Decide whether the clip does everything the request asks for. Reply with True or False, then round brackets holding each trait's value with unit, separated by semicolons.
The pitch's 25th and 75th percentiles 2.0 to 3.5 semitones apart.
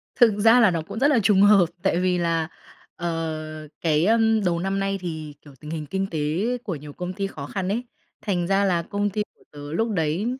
False (4.1 semitones)